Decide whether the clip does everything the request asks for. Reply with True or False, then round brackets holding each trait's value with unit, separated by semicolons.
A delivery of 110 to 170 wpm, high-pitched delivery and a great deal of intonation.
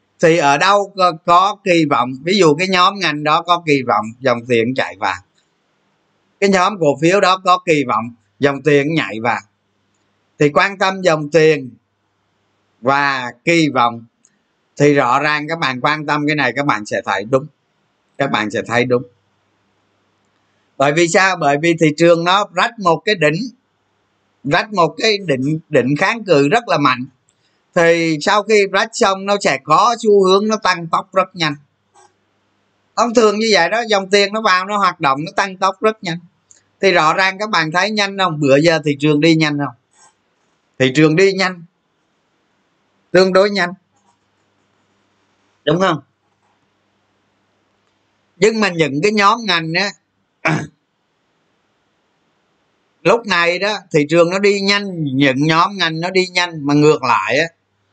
False (165 wpm; 155 Hz; 6.9 semitones)